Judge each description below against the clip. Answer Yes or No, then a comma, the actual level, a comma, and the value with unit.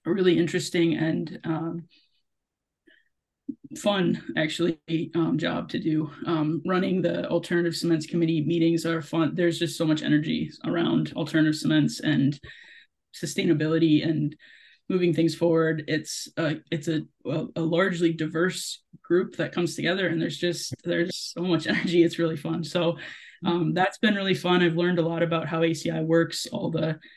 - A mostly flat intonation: Yes, narrow, 1.3 semitones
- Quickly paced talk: No, average, 160 wpm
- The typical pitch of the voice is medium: Yes, medium, 165 Hz